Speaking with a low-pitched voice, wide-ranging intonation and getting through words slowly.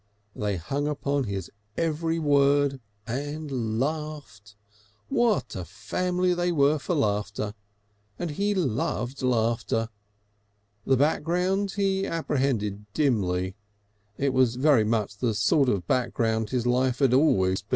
Yes: low, 130 Hz; wide, 5.8 semitones; slow, 125 wpm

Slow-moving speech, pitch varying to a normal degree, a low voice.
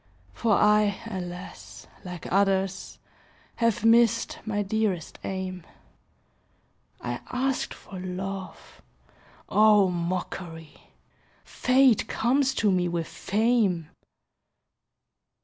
No: slow, 85 wpm; average, 3.8 semitones; high, 195 Hz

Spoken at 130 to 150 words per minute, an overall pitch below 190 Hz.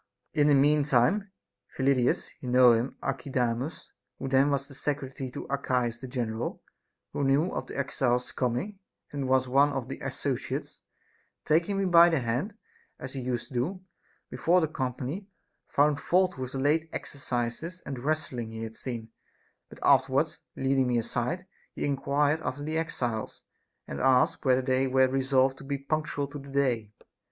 No: average, 165 wpm; low, 135 Hz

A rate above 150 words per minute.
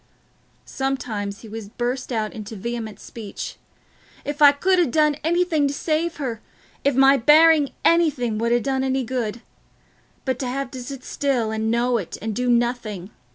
Yes: average, 165 wpm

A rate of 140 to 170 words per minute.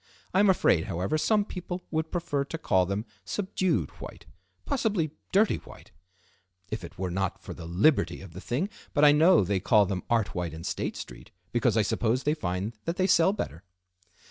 No: average, 195 wpm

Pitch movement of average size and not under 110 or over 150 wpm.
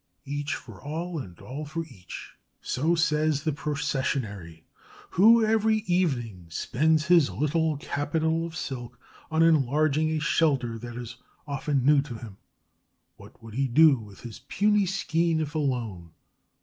Yes: average, 4.7 semitones; average, 145 wpm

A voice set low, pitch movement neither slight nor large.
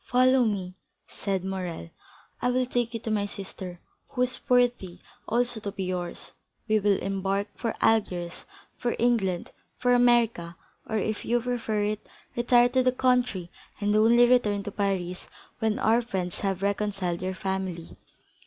No: high, 210 Hz; average, 4.2 semitones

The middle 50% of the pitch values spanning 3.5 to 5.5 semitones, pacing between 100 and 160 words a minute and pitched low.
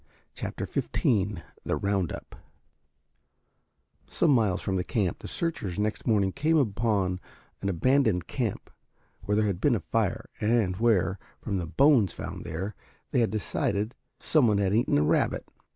Yes: average, 3.9 semitones; average, 150 wpm; low, 105 Hz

